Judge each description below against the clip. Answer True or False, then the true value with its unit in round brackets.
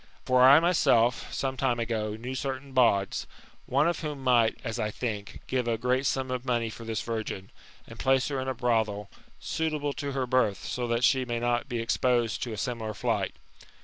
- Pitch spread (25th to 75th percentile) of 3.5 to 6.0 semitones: False (2.5 semitones)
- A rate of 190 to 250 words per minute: True (200 wpm)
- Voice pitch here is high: False (120 Hz)